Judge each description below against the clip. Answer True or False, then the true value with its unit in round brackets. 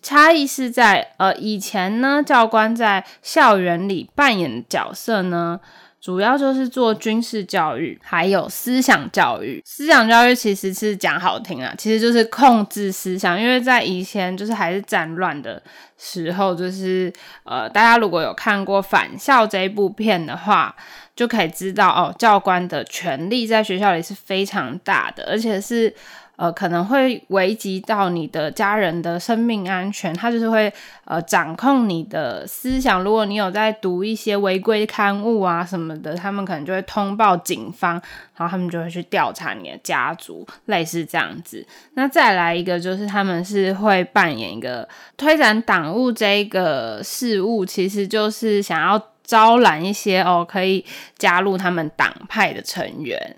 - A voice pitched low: False (200 Hz)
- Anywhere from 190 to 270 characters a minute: True (255 characters per minute)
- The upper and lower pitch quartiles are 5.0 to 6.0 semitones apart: False (3.6 semitones)